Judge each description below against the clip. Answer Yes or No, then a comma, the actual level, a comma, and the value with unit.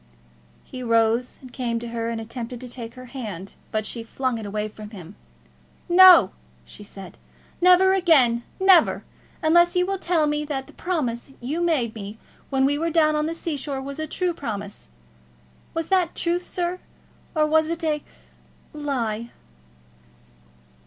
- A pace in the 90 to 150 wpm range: No, average, 160 wpm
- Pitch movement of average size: No, wide, 6.3 semitones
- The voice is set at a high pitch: Yes, very high, 270 Hz